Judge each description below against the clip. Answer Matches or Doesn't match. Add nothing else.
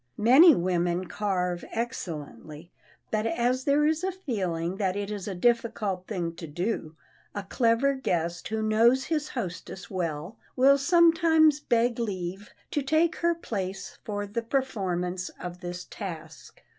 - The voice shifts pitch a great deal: Matches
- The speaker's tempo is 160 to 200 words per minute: Doesn't match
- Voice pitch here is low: Doesn't match